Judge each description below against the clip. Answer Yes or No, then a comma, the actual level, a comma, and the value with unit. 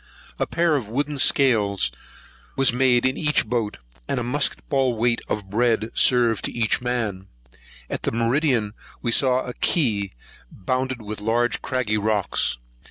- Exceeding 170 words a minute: No, average, 150 wpm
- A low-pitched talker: Yes, low, 120 Hz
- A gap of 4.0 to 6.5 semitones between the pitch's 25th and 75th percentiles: No, average, 3.4 semitones